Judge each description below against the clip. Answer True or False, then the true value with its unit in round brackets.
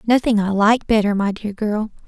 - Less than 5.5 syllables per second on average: True (5.0 syllables/s)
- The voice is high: True (215 Hz)